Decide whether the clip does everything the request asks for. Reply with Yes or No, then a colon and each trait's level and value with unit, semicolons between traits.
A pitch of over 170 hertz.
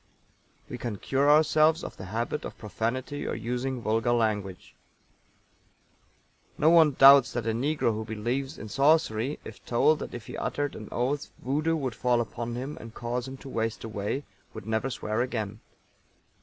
No: low, 120 Hz